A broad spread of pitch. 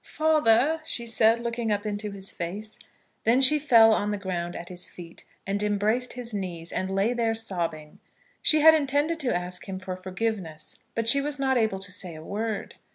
No: average, 4.4 semitones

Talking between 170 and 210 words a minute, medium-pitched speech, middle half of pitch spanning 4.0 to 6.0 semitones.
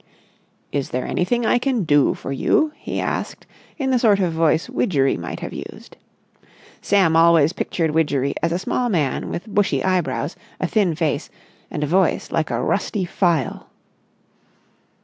No: average, 160 wpm; medium, 170 Hz; average, 5.1 semitones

